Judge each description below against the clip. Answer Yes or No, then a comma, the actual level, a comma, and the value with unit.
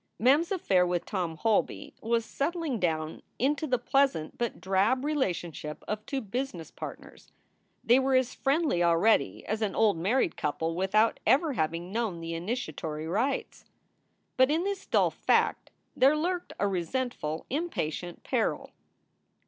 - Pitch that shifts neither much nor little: No, wide, 7.7 semitones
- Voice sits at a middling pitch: No, high, 220 Hz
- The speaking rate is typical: Yes, average, 150 wpm